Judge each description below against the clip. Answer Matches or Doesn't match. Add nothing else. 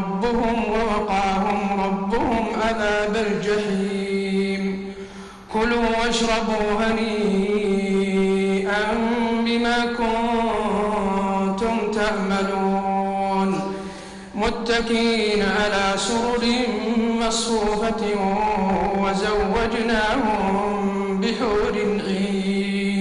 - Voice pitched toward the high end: Matches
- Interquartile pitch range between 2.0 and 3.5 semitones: Matches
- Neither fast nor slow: Doesn't match